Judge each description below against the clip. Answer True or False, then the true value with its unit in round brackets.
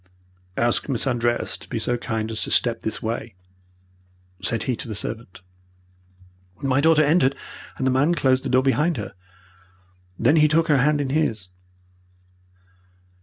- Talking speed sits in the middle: True (160 wpm)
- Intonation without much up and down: False (4.2 semitones)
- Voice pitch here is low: True (130 Hz)